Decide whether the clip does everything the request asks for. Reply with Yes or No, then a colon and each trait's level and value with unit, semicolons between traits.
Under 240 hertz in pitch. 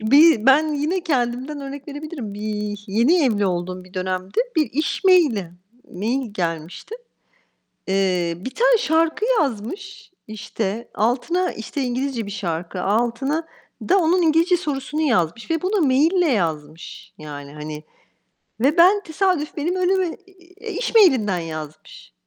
No: very high, 260 Hz